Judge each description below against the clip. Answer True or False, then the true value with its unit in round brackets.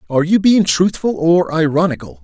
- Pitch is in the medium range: True (165 Hz)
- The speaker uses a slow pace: False (160 wpm)